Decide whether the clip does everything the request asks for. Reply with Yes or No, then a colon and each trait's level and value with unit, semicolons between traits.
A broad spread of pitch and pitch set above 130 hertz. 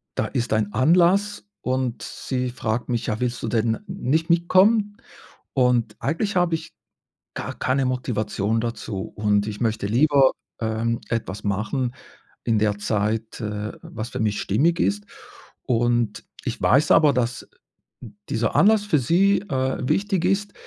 No: wide, 6.7 semitones; low, 120 Hz